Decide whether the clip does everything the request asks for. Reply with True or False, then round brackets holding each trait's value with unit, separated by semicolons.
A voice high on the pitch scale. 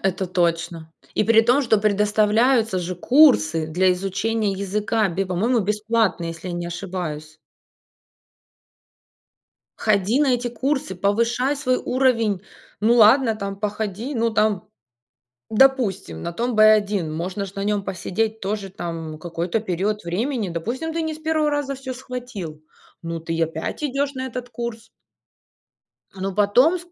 True (210 Hz)